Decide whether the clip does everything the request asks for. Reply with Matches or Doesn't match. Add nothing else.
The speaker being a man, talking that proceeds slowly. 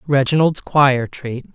Matches